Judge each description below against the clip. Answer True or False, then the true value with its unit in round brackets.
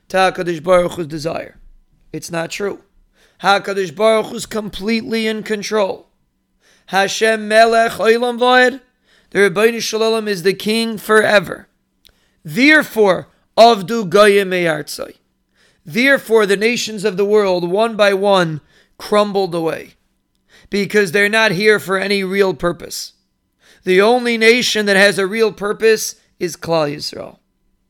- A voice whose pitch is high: True (210 Hz)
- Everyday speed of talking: False (120 wpm)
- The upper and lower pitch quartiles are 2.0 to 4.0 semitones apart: True (2.6 semitones)